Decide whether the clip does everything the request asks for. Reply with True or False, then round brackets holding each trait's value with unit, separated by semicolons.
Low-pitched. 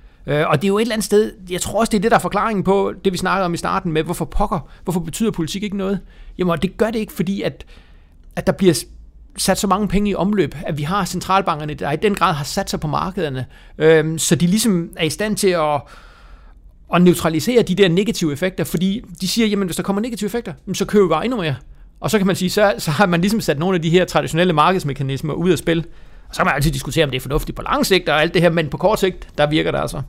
False (180 Hz)